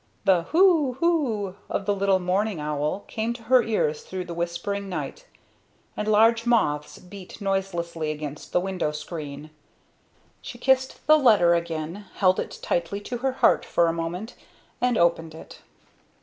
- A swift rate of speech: No, average, 155 wpm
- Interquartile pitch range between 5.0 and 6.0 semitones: Yes, average, 5.3 semitones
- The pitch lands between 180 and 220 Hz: Yes, high, 190 Hz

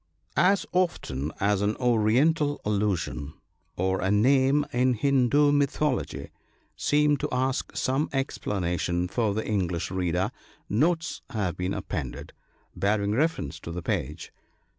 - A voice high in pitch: No, low, 110 Hz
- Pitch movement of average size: No, wide, 7.0 semitones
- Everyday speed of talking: No, slow, 125 wpm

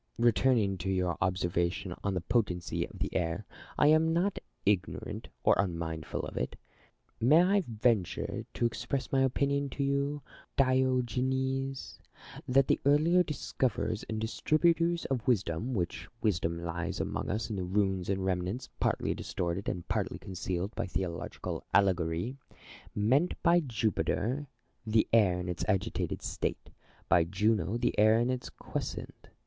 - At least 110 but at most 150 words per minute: Yes, average, 145 wpm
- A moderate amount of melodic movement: No, wide, 6.4 semitones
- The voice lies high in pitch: No, low, 110 Hz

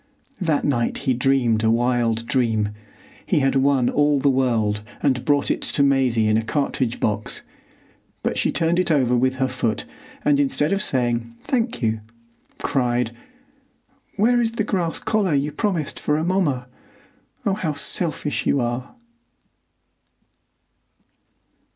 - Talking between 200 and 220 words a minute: No, average, 140 wpm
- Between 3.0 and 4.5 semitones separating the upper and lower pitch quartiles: No, average, 5.3 semitones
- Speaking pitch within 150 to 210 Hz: No, low, 135 Hz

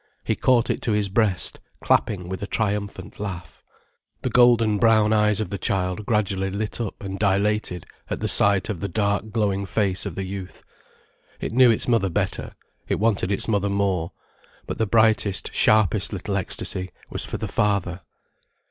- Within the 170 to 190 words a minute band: Yes, average, 175 wpm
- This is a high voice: No, low, 100 Hz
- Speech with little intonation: Yes, narrow, 2.1 semitones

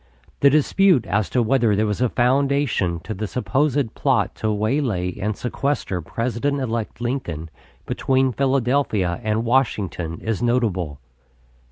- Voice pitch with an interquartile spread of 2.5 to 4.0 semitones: No, average, 4.7 semitones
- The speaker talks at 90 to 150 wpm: Yes, slow, 135 wpm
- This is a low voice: Yes, low, 115 Hz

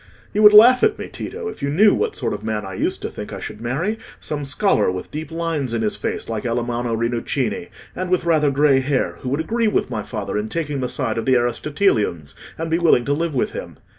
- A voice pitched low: No, medium, 145 Hz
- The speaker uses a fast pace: Yes, fast, 235 wpm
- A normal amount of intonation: No, wide, 6.4 semitones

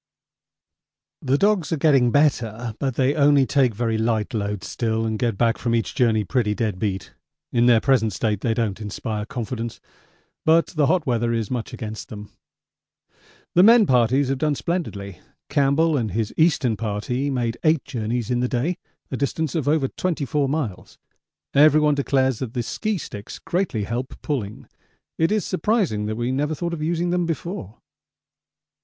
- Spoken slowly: No, average, 165 wpm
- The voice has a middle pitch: No, low, 125 Hz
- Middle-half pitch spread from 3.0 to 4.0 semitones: No, average, 5.3 semitones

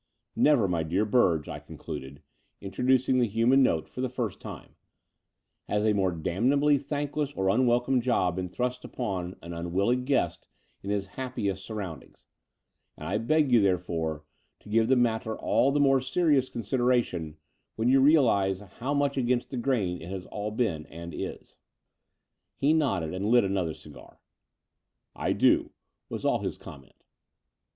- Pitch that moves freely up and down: Yes, wide, 5.9 semitones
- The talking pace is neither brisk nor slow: Yes, average, 160 wpm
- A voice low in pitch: Yes, low, 110 Hz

